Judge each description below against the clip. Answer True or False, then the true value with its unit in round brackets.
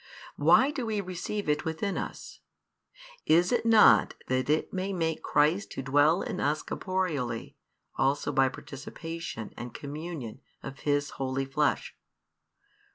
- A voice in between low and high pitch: True (155 Hz)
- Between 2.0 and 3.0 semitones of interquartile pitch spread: False (5.2 semitones)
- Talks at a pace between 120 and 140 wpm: True (135 wpm)